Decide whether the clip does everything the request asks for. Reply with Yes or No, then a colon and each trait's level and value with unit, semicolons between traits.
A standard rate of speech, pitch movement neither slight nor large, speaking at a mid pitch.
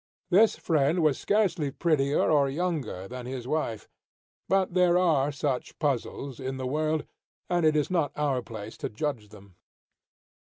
Yes: average, 155 wpm; average, 4.2 semitones; medium, 145 Hz